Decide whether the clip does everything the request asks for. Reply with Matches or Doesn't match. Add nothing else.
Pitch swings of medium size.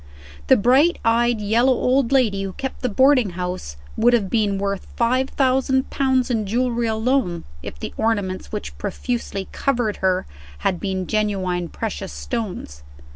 Matches